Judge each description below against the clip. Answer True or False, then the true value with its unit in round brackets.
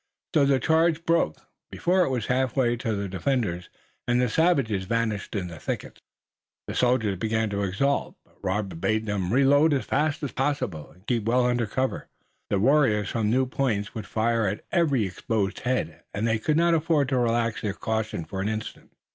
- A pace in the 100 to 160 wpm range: False (190 wpm)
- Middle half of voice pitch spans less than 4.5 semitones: False (4.8 semitones)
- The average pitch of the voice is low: True (115 Hz)